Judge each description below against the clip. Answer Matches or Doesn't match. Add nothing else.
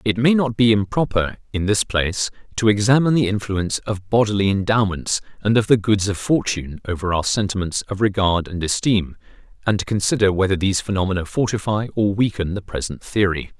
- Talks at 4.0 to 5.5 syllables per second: Doesn't match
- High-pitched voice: Doesn't match